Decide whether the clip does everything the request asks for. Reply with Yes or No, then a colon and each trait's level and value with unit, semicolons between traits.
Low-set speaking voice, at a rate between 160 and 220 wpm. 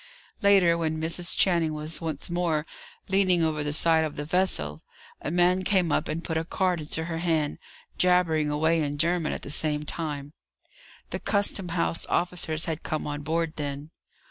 No: medium, 160 Hz; average, 175 wpm